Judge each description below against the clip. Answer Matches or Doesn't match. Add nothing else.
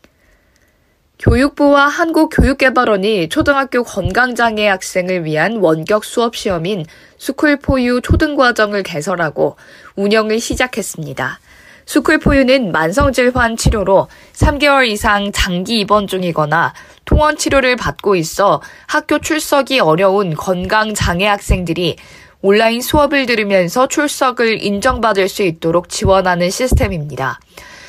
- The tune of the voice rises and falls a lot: Matches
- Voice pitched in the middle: Doesn't match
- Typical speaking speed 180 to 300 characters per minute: Matches